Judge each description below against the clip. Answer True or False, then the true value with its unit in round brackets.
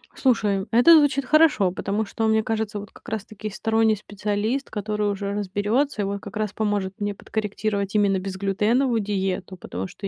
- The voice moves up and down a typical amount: False (1.9 semitones)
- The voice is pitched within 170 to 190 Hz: False (210 Hz)